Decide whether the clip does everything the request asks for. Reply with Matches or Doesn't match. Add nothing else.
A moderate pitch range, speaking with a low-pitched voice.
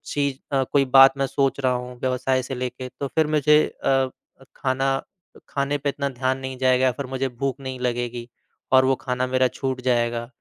Doesn't match